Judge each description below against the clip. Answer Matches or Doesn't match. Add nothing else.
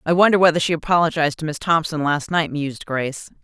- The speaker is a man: Doesn't match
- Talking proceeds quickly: Matches